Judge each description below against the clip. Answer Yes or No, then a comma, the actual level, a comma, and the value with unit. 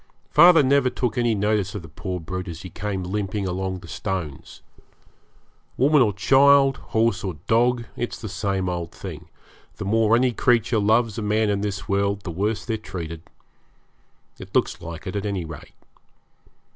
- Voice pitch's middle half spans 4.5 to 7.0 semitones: No, average, 3.7 semitones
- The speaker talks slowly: No, average, 170 wpm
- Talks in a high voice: No, low, 105 Hz